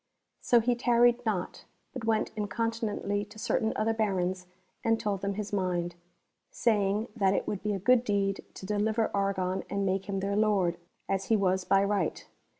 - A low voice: No, high, 205 Hz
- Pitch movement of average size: No, narrow, 2.3 semitones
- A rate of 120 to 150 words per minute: No, average, 175 wpm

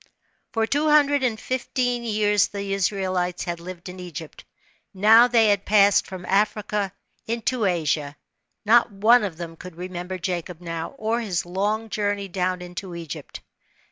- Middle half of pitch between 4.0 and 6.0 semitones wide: No, average, 3.6 semitones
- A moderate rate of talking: Yes, average, 155 wpm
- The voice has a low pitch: No, high, 195 Hz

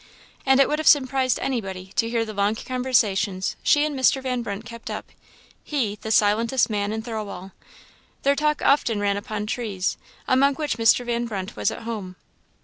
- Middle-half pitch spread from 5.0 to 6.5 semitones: No, average, 4.2 semitones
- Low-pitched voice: No, high, 230 Hz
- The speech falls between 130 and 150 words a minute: No, average, 180 wpm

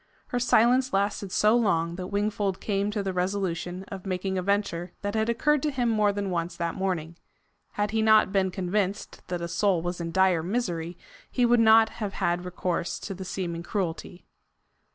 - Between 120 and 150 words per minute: No, average, 190 wpm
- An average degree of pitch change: Yes, average, 3.2 semitones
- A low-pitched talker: No, high, 195 Hz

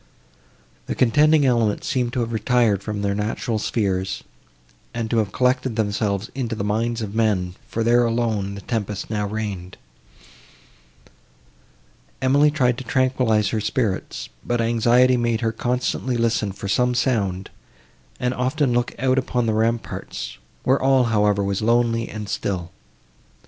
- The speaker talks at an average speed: Yes, average, 145 wpm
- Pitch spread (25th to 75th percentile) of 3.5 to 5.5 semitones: No, average, 3.1 semitones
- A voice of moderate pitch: No, low, 115 Hz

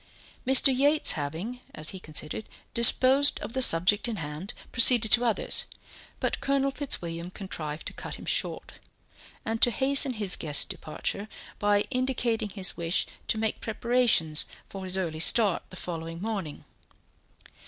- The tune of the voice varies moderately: No, wide, 6.7 semitones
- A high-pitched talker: Yes, high, 210 Hz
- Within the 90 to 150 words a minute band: Yes, average, 145 wpm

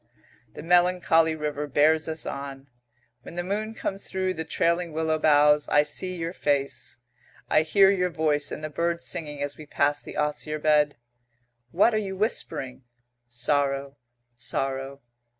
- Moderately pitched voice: Yes, medium, 155 Hz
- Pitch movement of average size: Yes, average, 3.2 semitones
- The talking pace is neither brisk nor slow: Yes, average, 150 wpm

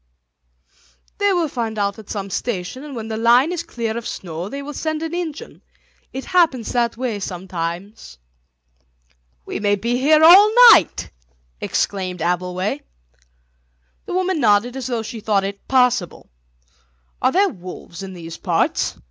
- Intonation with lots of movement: Yes, wide, 6.4 semitones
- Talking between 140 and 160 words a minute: Yes, average, 150 wpm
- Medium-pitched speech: No, high, 225 Hz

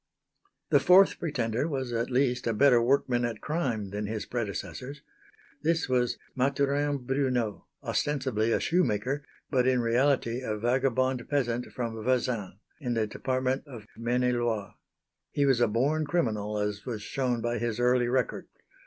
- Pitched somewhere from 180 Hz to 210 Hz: No, low, 125 Hz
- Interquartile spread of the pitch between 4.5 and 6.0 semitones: No, average, 2.9 semitones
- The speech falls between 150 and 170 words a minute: Yes, average, 155 wpm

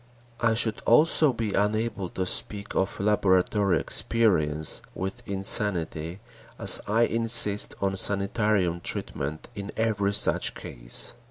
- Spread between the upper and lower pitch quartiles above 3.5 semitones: No, average, 3.0 semitones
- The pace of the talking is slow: Yes, slow, 115 wpm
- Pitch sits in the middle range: No, low, 100 Hz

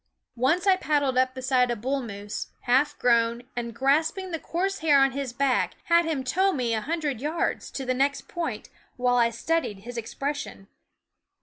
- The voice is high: Yes, very high, 265 Hz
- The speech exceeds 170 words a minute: Yes, average, 185 wpm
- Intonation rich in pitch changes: No, average, 4.5 semitones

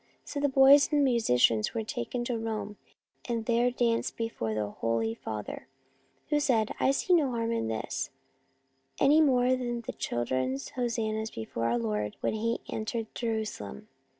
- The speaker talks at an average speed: Yes, average, 170 wpm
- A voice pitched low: No, high, 225 Hz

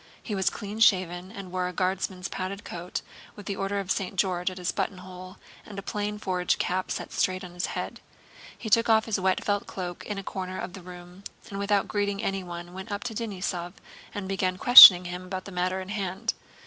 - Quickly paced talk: Yes, fast, 210 wpm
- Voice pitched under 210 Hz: Yes, high, 190 Hz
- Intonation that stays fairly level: Yes, narrow, 1.8 semitones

